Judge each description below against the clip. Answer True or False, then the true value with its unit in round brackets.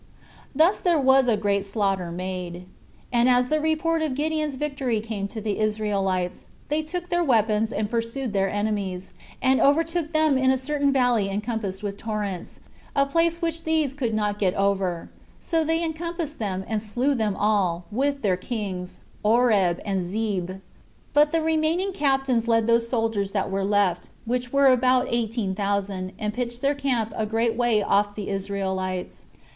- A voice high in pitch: True (225 Hz)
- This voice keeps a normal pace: True (170 wpm)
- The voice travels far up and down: True (5.7 semitones)